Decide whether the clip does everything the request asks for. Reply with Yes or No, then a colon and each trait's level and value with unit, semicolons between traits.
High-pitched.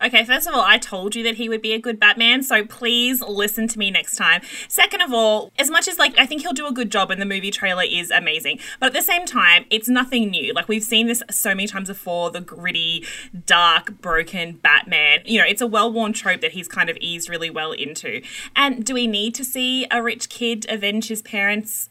Yes: high, 220 Hz